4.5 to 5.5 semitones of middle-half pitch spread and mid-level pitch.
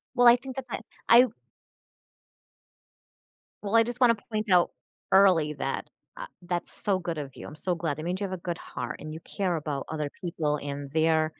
Yes: average, 4.8 semitones; medium, 175 Hz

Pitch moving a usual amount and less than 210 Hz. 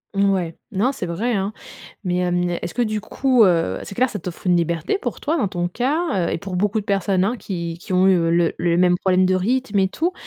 Yes: average, 3.5 semitones; high, 190 Hz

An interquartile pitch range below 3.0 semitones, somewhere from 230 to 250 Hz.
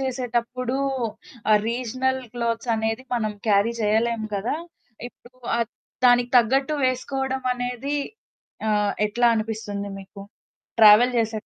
Yes: narrow, 2.6 semitones; high, 235 Hz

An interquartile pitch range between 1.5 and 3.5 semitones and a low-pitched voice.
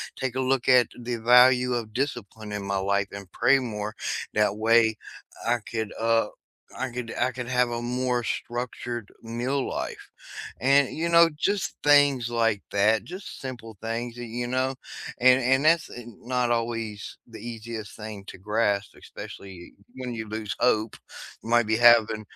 Yes: narrow, 2.5 semitones; low, 120 Hz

